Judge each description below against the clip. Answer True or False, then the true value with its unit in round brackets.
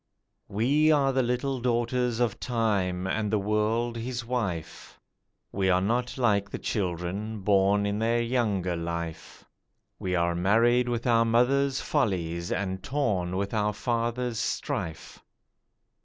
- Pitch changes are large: False (4.3 semitones)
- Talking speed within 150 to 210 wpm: False (135 wpm)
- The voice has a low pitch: True (110 Hz)